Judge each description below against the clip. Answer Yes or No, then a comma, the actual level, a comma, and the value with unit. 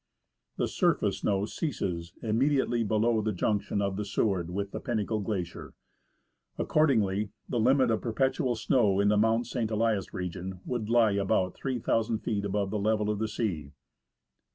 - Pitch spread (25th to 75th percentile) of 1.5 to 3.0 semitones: Yes, average, 2.7 semitones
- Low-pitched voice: Yes, low, 105 Hz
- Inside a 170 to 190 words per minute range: No, average, 155 wpm